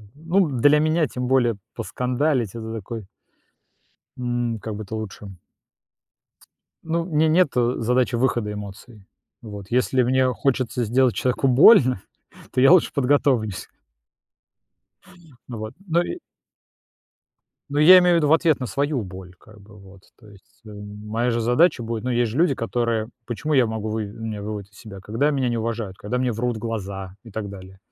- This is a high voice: No, low, 120 Hz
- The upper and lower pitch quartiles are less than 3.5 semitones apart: No, average, 3.8 semitones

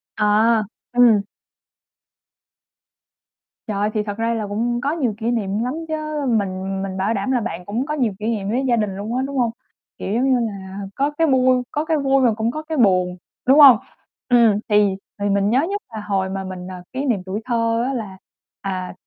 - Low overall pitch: No, high, 225 Hz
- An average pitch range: Yes, average, 4.3 semitones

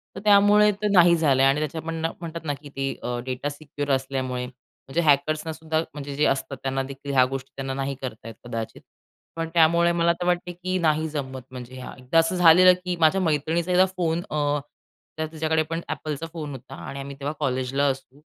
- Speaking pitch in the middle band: Yes, medium, 150 Hz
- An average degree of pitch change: Yes, average, 3.5 semitones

